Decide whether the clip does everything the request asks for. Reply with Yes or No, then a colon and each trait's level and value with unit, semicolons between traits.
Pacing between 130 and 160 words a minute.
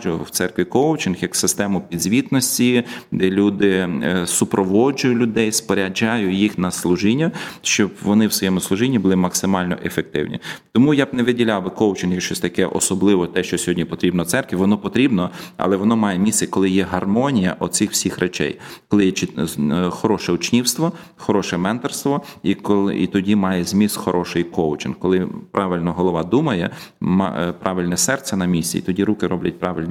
Yes: fast, 155 wpm